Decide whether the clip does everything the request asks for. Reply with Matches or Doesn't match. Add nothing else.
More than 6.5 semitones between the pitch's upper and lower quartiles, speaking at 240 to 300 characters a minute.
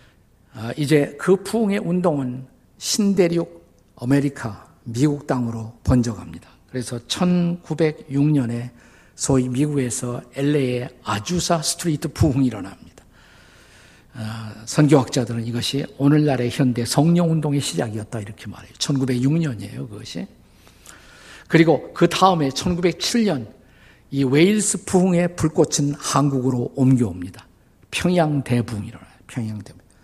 Doesn't match